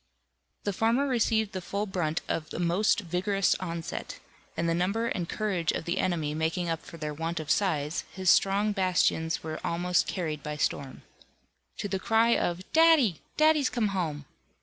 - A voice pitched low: No, medium, 180 Hz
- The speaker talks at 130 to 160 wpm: No, average, 170 wpm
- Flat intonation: No, average, 4.2 semitones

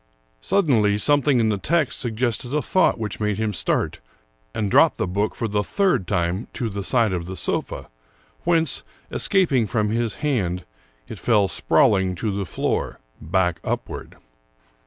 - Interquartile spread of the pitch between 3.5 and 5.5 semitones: Yes, average, 5.1 semitones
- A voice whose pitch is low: Yes, low, 110 Hz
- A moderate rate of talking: Yes, average, 155 wpm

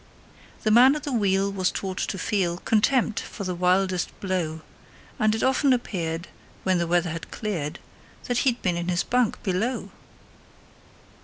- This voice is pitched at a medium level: No, high, 195 Hz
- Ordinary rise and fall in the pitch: Yes, average, 4.4 semitones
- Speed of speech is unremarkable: Yes, average, 160 wpm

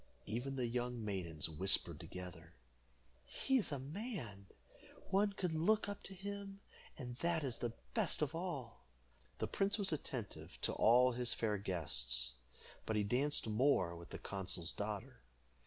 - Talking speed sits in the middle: Yes, average, 155 wpm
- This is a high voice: No, low, 125 Hz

